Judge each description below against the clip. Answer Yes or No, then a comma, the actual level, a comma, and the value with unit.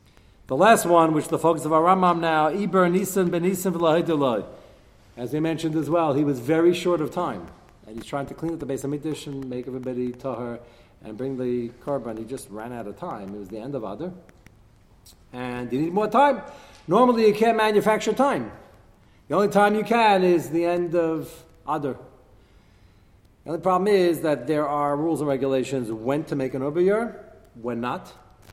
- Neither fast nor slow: Yes, average, 195 wpm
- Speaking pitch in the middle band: Yes, medium, 150 Hz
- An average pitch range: No, wide, 6.1 semitones